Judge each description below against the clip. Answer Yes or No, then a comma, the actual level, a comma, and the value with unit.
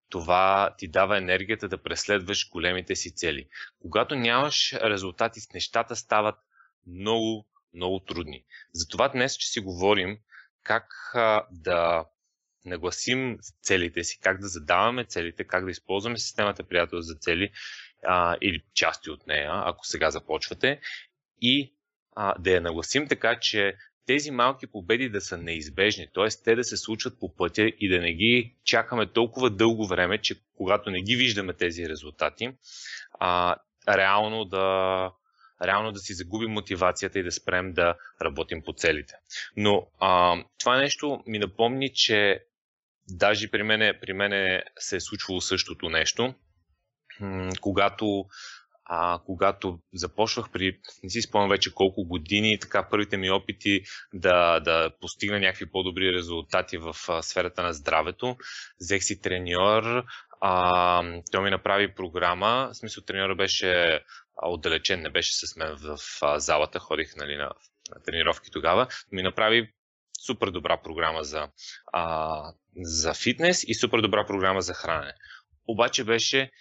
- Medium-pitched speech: No, very low, 95 Hz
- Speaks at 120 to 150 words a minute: Yes, average, 140 wpm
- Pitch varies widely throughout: No, average, 3.5 semitones